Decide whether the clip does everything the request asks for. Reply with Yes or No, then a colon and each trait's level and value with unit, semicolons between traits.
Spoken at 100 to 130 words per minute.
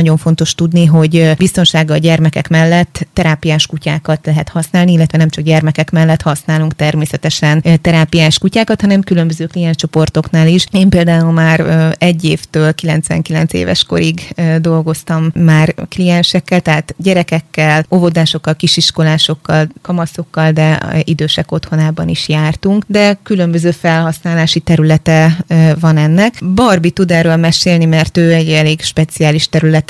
Yes: average, 125 wpm